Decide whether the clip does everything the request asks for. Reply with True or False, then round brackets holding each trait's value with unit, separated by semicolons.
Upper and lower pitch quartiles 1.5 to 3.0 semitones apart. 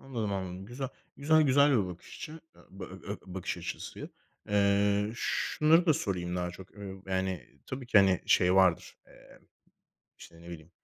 False (5.2 semitones)